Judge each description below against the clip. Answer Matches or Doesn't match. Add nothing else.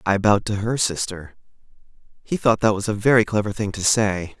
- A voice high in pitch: Doesn't match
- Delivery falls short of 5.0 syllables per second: Doesn't match